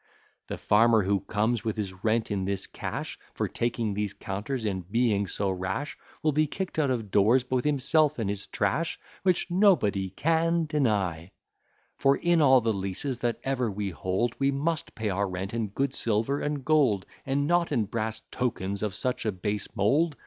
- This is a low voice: Yes, low, 115 Hz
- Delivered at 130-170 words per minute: No, average, 180 wpm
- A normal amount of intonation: No, wide, 5.7 semitones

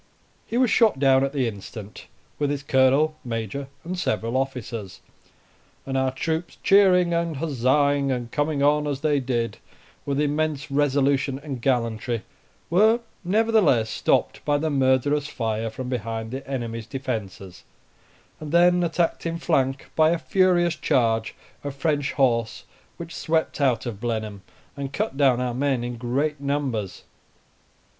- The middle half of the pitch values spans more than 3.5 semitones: Yes, average, 4.2 semitones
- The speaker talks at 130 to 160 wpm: Yes, average, 145 wpm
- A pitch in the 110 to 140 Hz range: Yes, low, 135 Hz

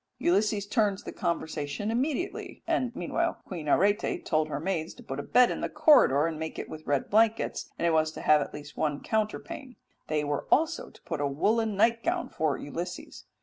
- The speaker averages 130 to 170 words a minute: No, average, 195 wpm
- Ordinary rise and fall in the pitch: No, wide, 7.0 semitones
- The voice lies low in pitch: No, high, 190 Hz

